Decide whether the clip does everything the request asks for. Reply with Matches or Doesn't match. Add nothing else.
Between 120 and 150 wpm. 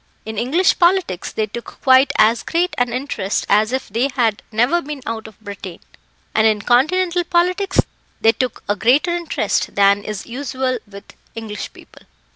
Doesn't match